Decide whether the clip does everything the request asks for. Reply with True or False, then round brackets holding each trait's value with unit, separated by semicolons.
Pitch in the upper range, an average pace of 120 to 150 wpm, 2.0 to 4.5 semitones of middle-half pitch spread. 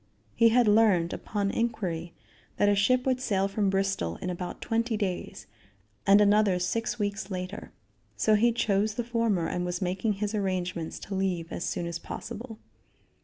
False (200 Hz; 170 wpm; 3.4 semitones)